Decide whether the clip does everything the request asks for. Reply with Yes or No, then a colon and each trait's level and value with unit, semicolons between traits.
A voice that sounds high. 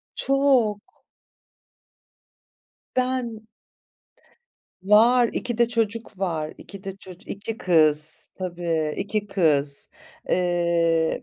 Yes: high, 195 Hz